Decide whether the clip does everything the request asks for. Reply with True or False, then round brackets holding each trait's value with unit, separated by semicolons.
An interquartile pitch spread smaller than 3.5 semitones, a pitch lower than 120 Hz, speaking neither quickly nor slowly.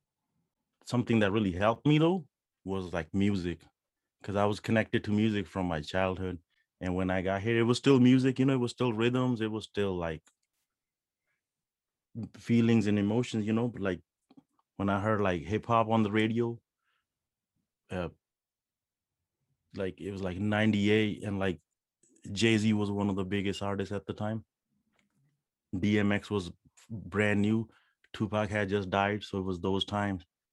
True (2.9 semitones; 105 Hz; 165 wpm)